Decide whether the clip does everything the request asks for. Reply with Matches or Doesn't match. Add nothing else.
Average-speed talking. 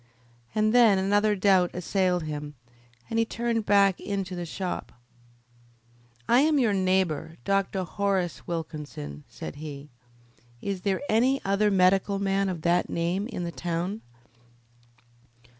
Doesn't match